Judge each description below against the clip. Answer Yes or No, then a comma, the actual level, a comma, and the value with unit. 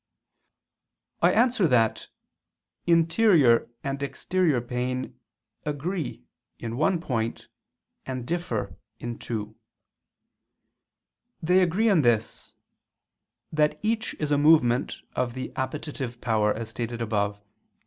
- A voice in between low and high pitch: No, low, 130 Hz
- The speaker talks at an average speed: No, slow, 105 wpm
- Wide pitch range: Yes, wide, 5.9 semitones